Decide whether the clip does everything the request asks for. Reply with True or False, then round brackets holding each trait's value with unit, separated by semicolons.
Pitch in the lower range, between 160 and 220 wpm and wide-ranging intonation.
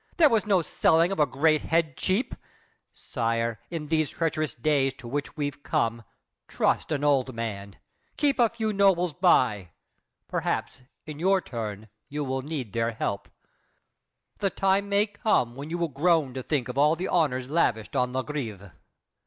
False (145 Hz; 170 wpm; 5.8 semitones)